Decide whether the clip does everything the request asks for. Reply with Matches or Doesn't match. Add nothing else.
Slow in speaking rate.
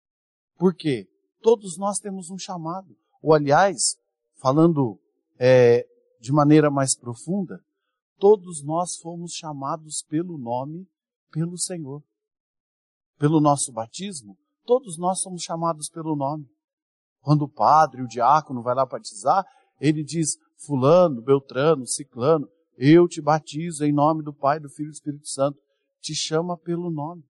Doesn't match